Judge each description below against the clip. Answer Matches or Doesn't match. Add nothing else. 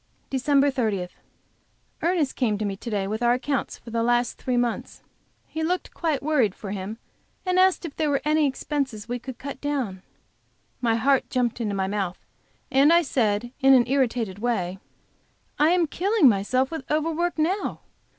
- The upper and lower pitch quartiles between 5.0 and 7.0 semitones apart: Matches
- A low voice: Doesn't match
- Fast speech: Doesn't match